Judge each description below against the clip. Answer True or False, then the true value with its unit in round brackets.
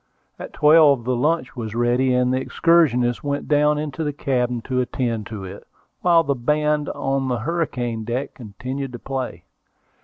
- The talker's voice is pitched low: True (130 Hz)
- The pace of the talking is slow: False (165 wpm)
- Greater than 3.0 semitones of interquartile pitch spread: True (3.6 semitones)